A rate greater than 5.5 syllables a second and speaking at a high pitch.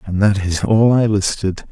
No: 5.9 syllables/s; low, 100 Hz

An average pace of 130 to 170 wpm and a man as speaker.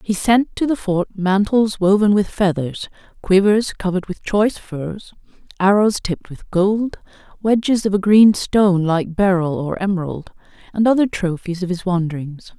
No: average, 155 wpm; female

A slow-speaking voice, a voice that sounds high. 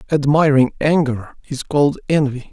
No: slow, 120 wpm; medium, 140 Hz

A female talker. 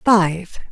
Yes: female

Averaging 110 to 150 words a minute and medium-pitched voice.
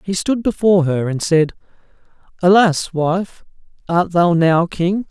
Yes: average, 140 wpm; medium, 175 Hz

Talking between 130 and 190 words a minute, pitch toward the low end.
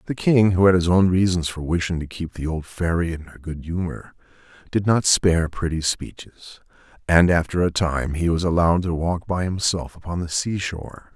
No: fast, 205 wpm; very low, 85 Hz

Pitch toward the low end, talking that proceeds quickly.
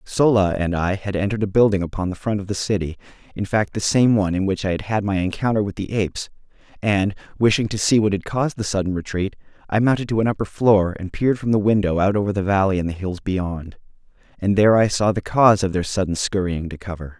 Yes: low, 100 Hz; fast, 240 wpm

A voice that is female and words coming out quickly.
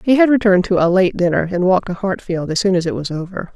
Yes: female; fast, 285 wpm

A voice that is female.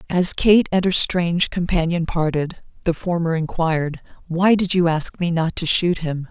Yes: female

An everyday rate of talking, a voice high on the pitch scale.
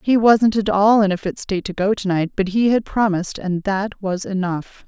No: fast, 245 wpm; high, 200 Hz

